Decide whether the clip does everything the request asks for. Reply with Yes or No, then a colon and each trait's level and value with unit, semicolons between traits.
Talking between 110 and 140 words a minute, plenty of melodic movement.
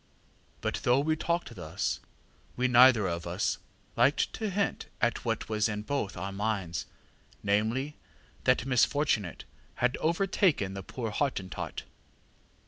Yes: slow, 135 wpm; wide, 5.9 semitones